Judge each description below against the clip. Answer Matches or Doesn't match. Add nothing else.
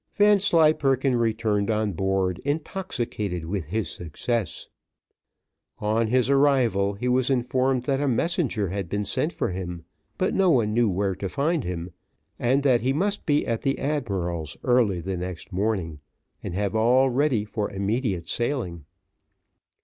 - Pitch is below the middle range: Matches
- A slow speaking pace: Doesn't match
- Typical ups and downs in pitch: Doesn't match